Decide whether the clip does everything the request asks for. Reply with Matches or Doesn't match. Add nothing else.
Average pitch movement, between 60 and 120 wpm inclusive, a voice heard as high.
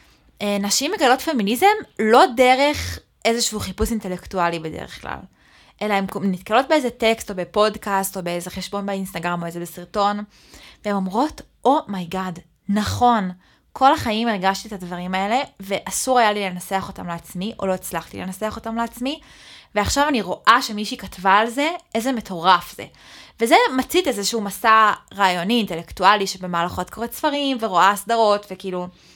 Doesn't match